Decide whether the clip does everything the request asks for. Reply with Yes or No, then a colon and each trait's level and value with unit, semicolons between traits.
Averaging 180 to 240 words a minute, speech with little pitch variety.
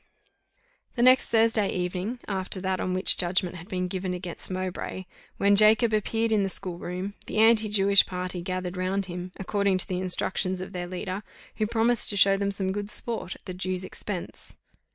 Yes: average, 190 wpm; narrow, 2.3 semitones